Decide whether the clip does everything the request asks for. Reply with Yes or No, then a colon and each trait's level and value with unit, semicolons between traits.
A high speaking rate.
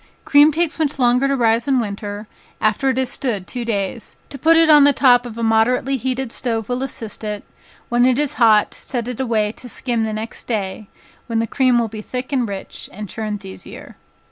Yes: fast, 215 wpm